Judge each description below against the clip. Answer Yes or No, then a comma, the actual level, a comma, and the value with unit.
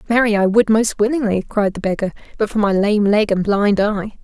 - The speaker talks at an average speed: No, fast, 225 wpm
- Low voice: No, high, 210 Hz